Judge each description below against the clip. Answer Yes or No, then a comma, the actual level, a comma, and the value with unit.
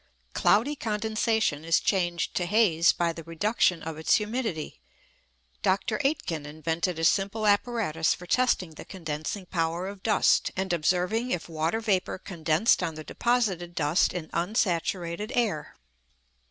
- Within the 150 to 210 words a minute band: No, average, 140 wpm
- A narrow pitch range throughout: No, average, 4.8 semitones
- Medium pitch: Yes, medium, 180 Hz